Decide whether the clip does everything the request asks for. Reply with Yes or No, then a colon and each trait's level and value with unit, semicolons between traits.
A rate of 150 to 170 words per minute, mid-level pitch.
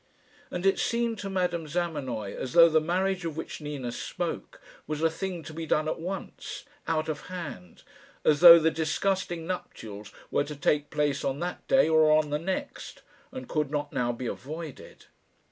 No: average, 180 wpm; medium, 160 Hz